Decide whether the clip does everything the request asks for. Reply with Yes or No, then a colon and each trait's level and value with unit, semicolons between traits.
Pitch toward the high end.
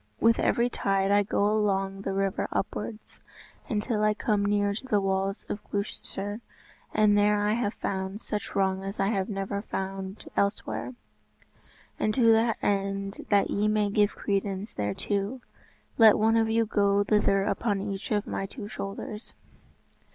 Yes: high, 205 Hz